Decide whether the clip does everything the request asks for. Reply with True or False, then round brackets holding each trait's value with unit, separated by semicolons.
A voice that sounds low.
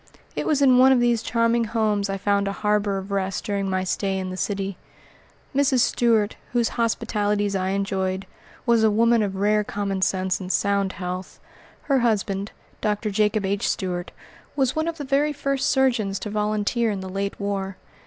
False (205 Hz)